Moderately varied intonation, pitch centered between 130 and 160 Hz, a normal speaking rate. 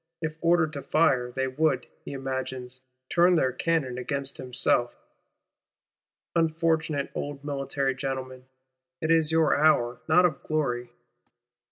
No: average, 3.5 semitones; medium, 140 Hz; slow, 125 wpm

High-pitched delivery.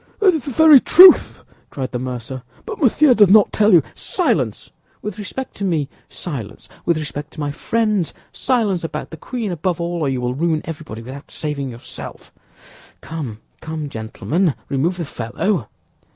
No: medium, 165 Hz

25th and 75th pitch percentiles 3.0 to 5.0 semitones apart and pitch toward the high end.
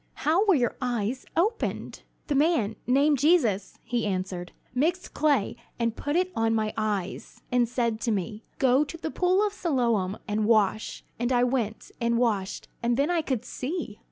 No: wide, 5.6 semitones; high, 245 Hz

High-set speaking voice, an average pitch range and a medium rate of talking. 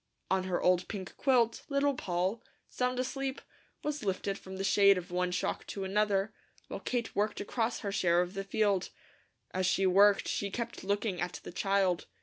Yes: high, 200 Hz; average, 3.2 semitones; average, 180 wpm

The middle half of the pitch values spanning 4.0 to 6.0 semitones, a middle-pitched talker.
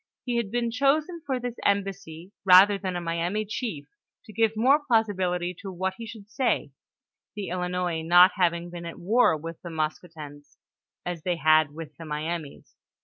Yes: average, 4.6 semitones; medium, 180 Hz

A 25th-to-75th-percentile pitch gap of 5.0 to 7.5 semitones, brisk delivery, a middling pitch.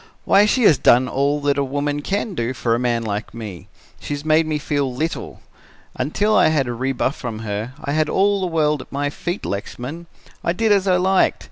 Yes: average, 5.3 semitones; fast, 220 wpm; medium, 145 Hz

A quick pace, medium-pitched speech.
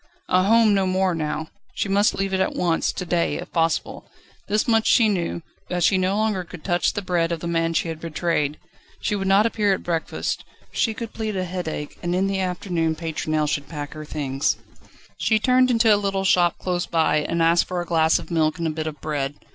Yes: fast, 225 wpm; medium, 175 Hz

